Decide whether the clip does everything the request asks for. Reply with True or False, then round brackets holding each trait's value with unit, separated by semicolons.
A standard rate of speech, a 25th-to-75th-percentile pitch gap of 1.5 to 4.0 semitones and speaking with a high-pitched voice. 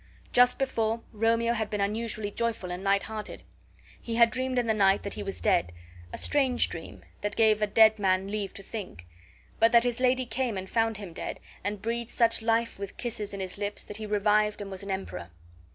False (215 wpm; 2.6 semitones; 215 Hz)